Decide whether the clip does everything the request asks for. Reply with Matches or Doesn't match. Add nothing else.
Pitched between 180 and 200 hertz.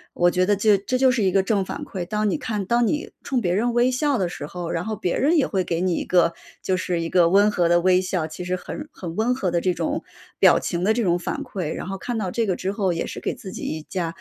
Matches